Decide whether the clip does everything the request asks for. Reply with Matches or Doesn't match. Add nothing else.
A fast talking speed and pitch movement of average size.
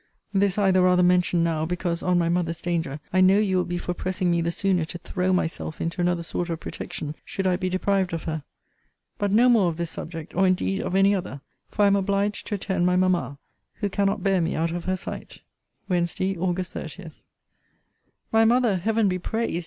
Doesn't match